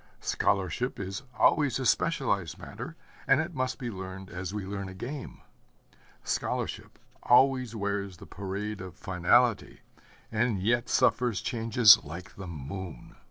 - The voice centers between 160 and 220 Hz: No, low, 105 Hz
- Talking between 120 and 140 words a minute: Yes, slow, 135 wpm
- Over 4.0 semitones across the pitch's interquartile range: Yes, average, 4.7 semitones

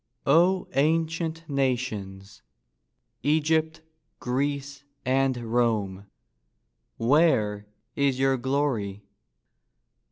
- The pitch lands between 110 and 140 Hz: Yes, low, 135 Hz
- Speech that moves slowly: Yes, slow, 60 wpm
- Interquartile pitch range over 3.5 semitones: Yes, wide, 5.4 semitones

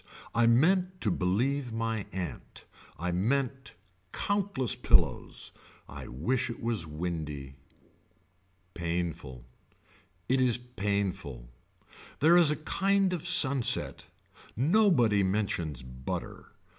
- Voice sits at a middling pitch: No, low, 115 Hz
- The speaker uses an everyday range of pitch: No, wide, 8.3 semitones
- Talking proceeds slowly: Yes, slow, 100 wpm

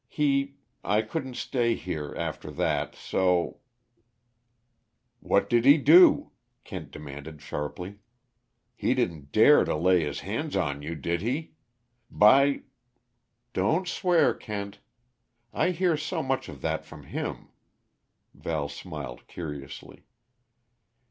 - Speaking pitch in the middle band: No, low, 105 Hz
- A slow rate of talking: Yes, slow, 120 wpm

